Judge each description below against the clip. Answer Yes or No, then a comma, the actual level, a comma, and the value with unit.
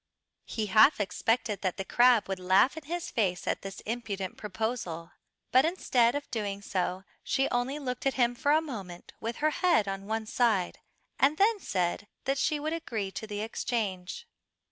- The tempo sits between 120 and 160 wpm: No, average, 180 wpm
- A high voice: Yes, high, 225 Hz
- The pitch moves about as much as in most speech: No, wide, 5.7 semitones